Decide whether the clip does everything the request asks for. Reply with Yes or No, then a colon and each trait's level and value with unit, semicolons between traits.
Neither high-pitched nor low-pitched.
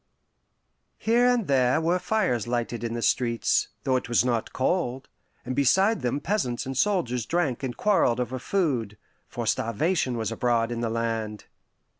No: low, 125 Hz